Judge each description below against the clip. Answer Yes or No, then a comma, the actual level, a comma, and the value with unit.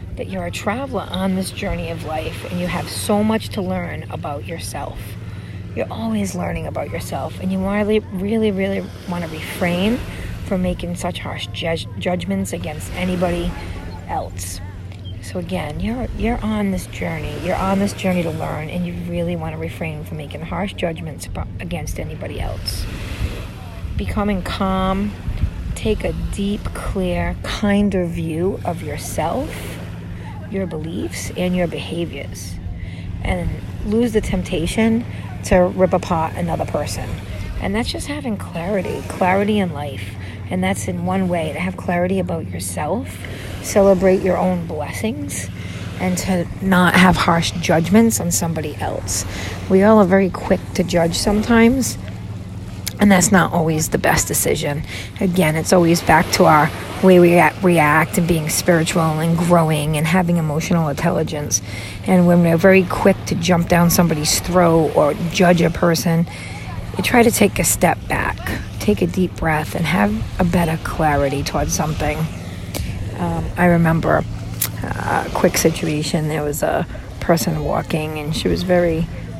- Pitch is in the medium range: Yes, medium, 150 Hz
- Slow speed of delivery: No, average, 150 wpm